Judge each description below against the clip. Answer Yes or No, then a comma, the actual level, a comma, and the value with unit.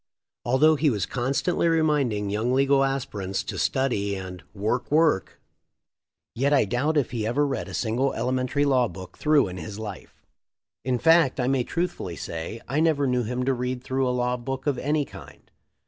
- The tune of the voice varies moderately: Yes, average, 4.3 semitones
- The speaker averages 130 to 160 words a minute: No, average, 180 wpm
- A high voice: No, low, 125 Hz